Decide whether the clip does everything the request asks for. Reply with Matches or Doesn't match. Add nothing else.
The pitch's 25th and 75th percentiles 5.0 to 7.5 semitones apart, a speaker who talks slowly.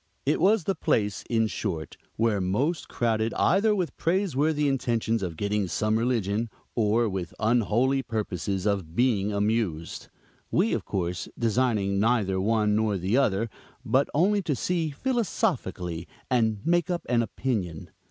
Doesn't match